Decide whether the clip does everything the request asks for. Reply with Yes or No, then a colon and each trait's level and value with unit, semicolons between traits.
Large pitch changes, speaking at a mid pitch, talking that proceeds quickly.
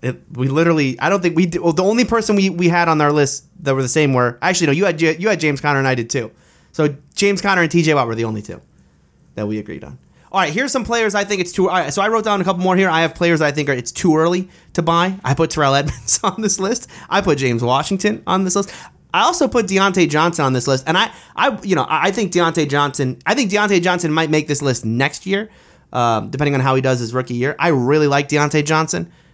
Yes: wide, 5.7 semitones; medium, 160 Hz; fast, 270 wpm